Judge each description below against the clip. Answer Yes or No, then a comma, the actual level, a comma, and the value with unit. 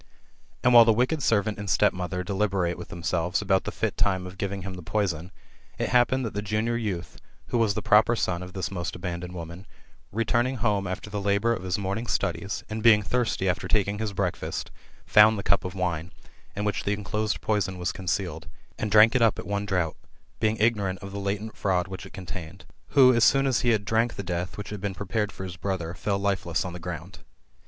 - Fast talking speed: Yes, fast, 220 wpm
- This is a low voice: Yes, low, 100 Hz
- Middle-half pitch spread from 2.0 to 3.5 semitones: Yes, average, 2.9 semitones